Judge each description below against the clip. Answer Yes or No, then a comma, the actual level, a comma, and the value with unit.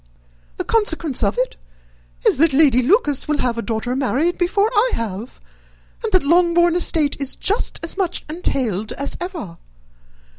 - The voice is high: Yes, very high, 300 Hz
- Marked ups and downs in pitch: Yes, wide, 6.0 semitones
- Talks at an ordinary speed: Yes, average, 155 wpm